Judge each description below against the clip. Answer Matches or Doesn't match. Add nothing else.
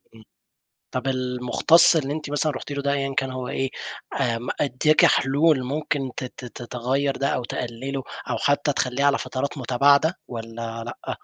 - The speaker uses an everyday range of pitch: Doesn't match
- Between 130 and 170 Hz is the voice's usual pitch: Matches